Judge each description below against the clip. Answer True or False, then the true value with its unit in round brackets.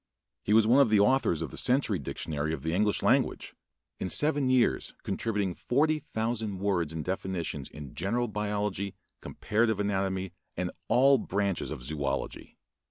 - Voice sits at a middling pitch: False (100 Hz)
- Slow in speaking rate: False (150 wpm)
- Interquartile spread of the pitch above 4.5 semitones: True (5.0 semitones)